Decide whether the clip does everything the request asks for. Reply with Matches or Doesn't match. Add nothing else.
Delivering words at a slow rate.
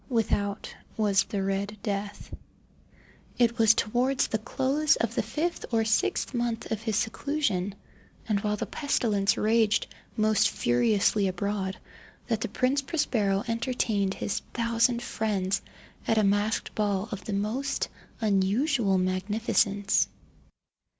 Matches